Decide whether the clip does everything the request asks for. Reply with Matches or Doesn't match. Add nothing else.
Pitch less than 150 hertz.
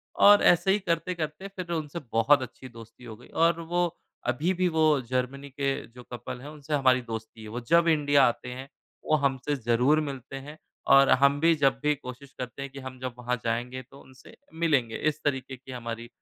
Matches